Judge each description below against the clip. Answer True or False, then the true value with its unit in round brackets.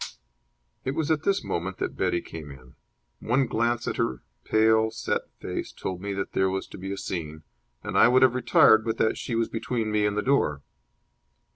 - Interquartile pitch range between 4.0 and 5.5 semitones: True (4.5 semitones)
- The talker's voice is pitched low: True (110 Hz)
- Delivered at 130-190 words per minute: False (205 wpm)